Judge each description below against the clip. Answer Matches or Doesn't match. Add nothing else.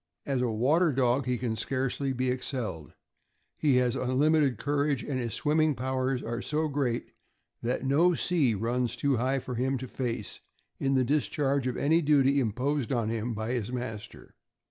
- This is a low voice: Matches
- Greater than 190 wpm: Doesn't match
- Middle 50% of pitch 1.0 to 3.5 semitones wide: Matches